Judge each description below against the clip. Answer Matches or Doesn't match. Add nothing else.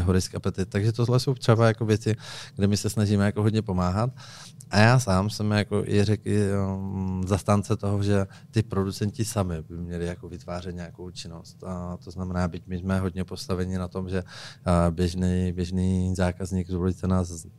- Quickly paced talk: Matches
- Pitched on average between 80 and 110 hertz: Matches